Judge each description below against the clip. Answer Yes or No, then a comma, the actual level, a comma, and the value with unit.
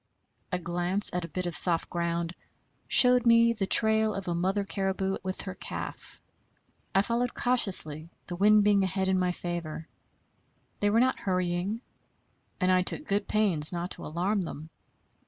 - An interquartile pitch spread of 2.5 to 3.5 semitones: Yes, average, 3.1 semitones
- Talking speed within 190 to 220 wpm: No, average, 165 wpm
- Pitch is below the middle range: No, high, 190 Hz